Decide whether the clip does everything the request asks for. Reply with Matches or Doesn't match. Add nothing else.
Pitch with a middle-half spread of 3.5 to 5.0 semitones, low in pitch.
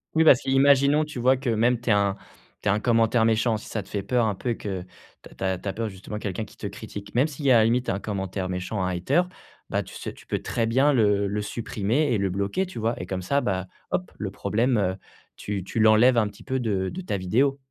Matches